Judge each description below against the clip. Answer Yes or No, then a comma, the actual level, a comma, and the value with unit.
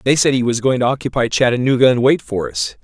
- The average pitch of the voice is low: Yes, low, 120 Hz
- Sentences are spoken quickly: Yes, fast, 255 wpm